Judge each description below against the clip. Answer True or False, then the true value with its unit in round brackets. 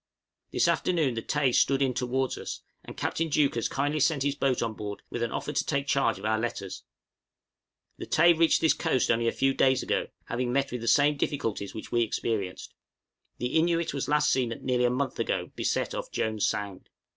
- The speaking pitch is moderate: False (130 Hz)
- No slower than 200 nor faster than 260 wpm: True (205 wpm)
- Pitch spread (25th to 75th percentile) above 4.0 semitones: False (3.7 semitones)